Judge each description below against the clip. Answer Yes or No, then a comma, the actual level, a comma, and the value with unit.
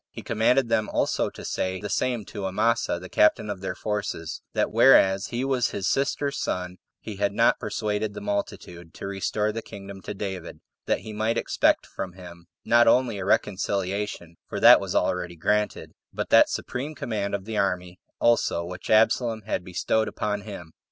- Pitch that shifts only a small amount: No, average, 3.2 semitones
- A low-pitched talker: Yes, low, 105 Hz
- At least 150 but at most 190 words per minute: Yes, average, 180 wpm